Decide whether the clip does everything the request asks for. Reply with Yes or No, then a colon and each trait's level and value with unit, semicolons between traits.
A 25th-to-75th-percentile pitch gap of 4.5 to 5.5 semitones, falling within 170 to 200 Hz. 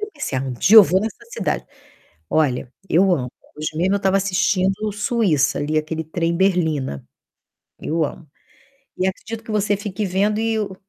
Yes: average, 4.8 semitones; high, 190 Hz